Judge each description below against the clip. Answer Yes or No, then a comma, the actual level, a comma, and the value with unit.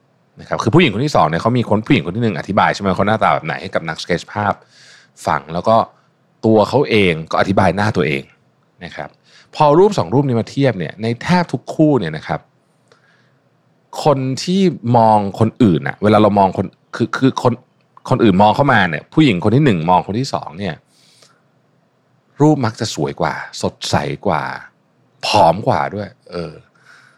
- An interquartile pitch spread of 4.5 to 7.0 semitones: Yes, average, 4.9 semitones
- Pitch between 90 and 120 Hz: Yes, low, 115 Hz